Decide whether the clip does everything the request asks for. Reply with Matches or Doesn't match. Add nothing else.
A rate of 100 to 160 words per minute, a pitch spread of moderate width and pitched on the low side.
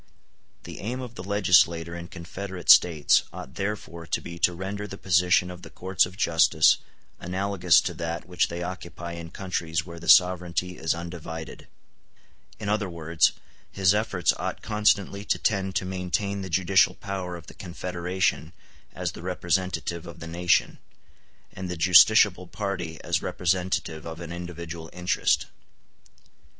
Doesn't match